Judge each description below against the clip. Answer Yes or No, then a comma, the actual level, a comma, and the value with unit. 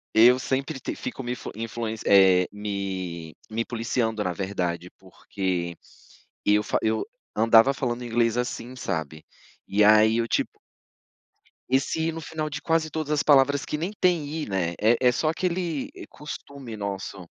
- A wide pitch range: Yes, wide, 6.2 semitones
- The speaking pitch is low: Yes, low, 115 Hz